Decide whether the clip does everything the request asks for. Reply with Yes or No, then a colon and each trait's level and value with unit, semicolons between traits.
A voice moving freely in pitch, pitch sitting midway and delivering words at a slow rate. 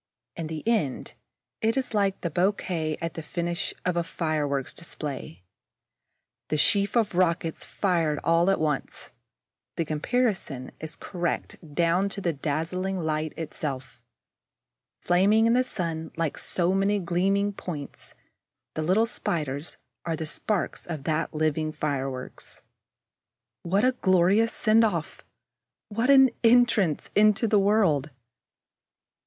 No: average, 4.5 semitones; medium, 175 Hz; slow, 130 wpm